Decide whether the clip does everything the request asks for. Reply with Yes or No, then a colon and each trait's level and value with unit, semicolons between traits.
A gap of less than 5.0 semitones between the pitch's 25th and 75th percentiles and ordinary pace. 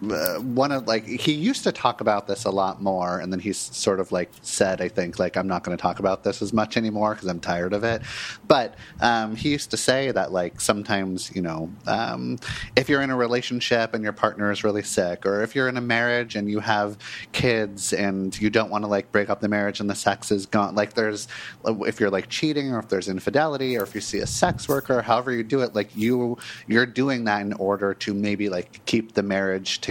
No: average, 3.4 semitones; fast, 245 wpm